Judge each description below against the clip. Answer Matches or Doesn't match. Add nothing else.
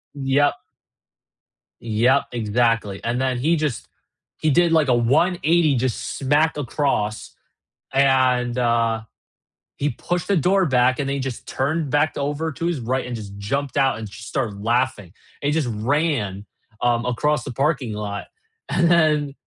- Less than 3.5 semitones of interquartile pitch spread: Doesn't match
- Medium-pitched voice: Doesn't match